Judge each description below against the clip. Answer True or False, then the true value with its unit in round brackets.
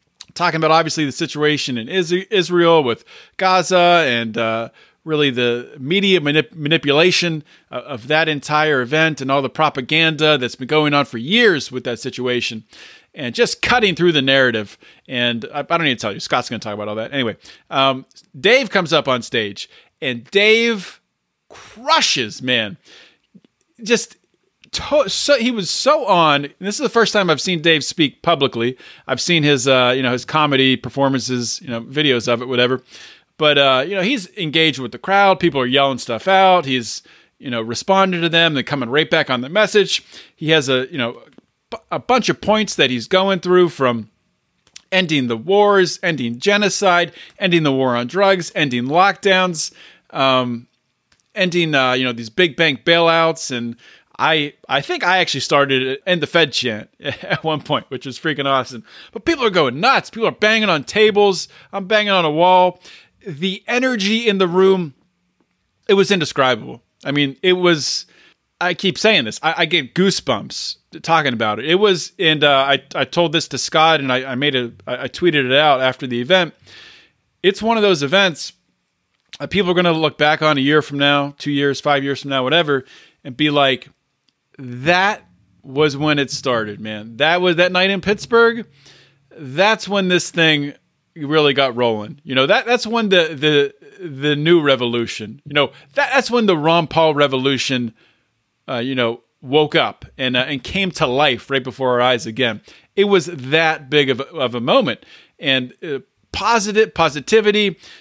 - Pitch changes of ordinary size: False (5.7 semitones)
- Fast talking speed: False (185 wpm)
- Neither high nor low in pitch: True (150 Hz)